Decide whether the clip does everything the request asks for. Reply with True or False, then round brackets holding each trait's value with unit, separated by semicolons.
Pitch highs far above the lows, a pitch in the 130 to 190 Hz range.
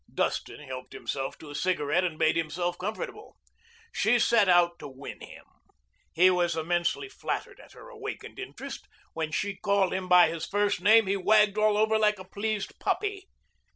False (3.8 semitones; 185 Hz)